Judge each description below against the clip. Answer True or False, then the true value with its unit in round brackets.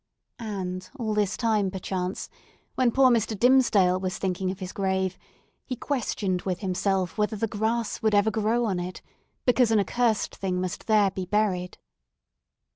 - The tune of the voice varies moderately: True (3.1 semitones)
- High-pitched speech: True (205 Hz)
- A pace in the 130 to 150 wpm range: False (160 wpm)